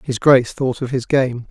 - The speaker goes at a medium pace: No, fast, 240 wpm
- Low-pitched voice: Yes, low, 130 Hz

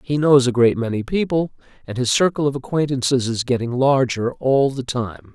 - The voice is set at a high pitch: No, low, 130 Hz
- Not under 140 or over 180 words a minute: No, average, 190 wpm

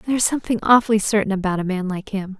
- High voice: Yes, high, 205 Hz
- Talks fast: Yes, fast, 250 wpm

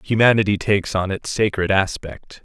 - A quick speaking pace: No, average, 150 wpm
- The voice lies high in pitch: No, low, 100 Hz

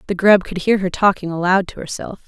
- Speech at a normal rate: No, fast, 235 wpm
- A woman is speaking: Yes, female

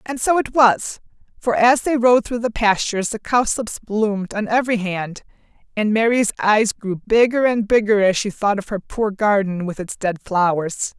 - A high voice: Yes, high, 215 Hz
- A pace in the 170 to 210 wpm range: Yes, average, 190 wpm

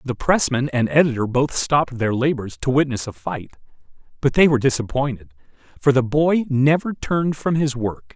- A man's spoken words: Yes, male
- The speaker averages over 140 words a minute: Yes, average, 175 wpm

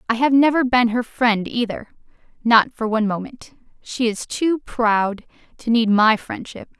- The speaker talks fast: No, average, 170 wpm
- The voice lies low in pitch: No, high, 235 Hz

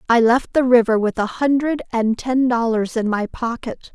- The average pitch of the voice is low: No, high, 240 Hz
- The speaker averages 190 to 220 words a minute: Yes, average, 200 wpm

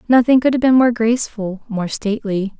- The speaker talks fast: No, average, 185 wpm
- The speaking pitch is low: No, high, 225 Hz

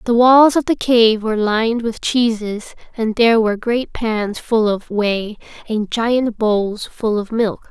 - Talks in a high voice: Yes, high, 225 Hz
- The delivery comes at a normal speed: Yes, average, 180 wpm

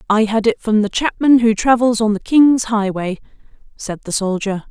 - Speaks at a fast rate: No, average, 190 wpm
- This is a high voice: Yes, high, 220 Hz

